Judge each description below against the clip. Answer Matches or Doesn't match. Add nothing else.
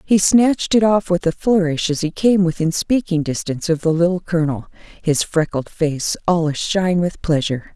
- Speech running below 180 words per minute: Doesn't match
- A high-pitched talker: Doesn't match